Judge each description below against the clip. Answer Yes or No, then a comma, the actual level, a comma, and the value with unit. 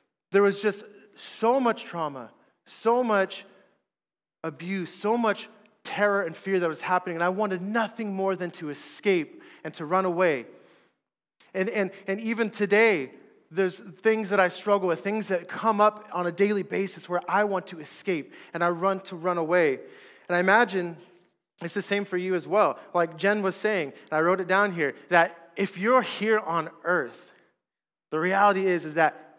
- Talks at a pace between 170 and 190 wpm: Yes, average, 185 wpm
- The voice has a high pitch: Yes, high, 195 Hz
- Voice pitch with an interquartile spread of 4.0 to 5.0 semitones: No, average, 3.1 semitones